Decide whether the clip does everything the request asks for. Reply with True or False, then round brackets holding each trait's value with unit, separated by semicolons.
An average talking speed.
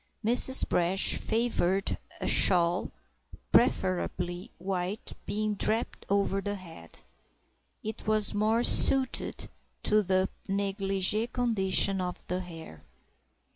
False (95 wpm)